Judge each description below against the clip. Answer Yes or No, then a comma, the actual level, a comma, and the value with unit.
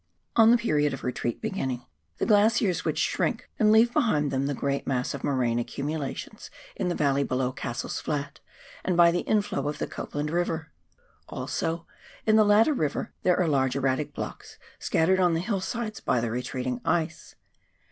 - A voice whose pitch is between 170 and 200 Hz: No, medium, 155 Hz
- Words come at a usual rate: Yes, average, 180 wpm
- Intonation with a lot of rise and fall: Yes, wide, 6.8 semitones